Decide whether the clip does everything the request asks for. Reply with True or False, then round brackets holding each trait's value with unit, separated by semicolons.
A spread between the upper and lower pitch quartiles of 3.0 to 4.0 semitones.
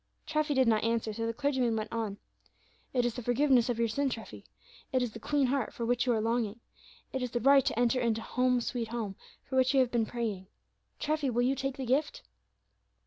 False (2.6 semitones)